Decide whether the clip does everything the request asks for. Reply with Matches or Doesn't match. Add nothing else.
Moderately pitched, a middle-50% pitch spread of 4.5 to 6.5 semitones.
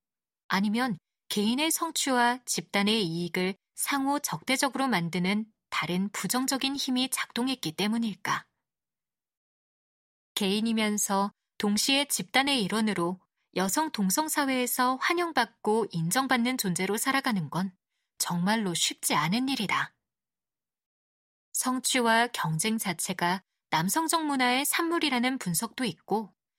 Doesn't match